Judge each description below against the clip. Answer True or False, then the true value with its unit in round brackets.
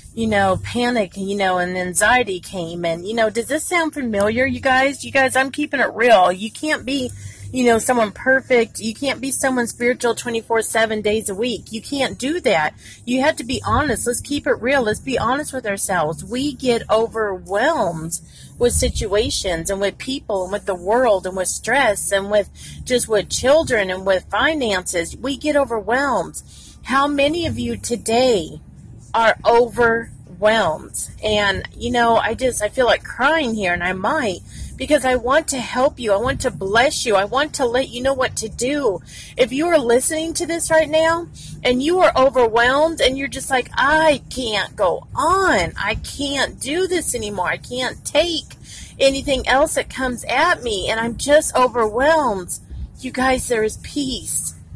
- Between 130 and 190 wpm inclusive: True (180 wpm)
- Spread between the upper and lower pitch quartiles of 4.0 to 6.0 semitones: True (4.9 semitones)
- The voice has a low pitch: False (245 Hz)